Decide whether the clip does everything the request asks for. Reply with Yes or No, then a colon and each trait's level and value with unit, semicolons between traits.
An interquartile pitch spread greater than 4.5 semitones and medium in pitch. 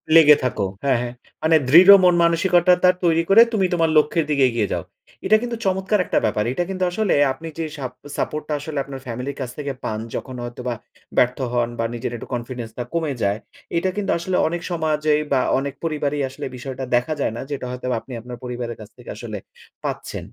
Yes: average, 5.3 semitones; medium, 145 Hz